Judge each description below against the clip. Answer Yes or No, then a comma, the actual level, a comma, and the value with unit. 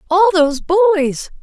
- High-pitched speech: Yes, very high, 350 Hz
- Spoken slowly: Yes, slow, 125 wpm